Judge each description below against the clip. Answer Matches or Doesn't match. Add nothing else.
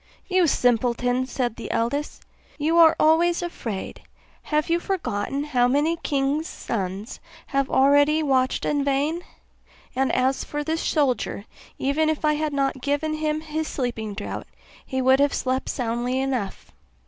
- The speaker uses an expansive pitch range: Doesn't match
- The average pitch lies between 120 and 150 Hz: Doesn't match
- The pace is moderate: Matches